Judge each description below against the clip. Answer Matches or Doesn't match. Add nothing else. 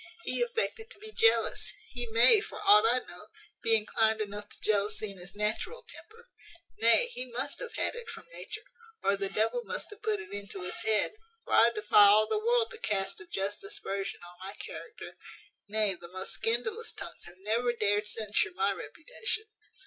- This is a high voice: Matches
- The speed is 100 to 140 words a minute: Doesn't match